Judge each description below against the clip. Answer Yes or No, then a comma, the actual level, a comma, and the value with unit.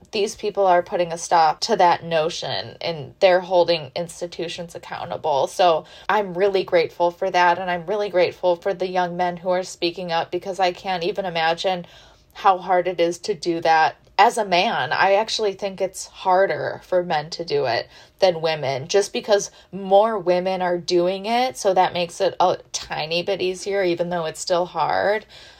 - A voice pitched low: No, medium, 180 Hz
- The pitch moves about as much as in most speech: No, narrow, 2.1 semitones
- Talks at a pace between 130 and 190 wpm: Yes, average, 185 wpm